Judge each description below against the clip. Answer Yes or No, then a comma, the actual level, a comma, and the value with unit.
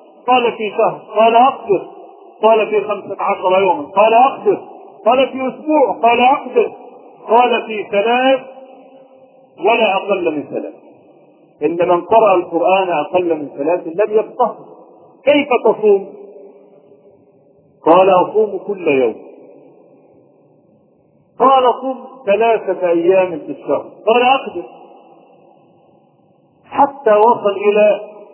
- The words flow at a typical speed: Yes, average, 105 wpm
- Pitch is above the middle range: Yes, high, 220 Hz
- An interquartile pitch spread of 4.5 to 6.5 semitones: Yes, wide, 5.4 semitones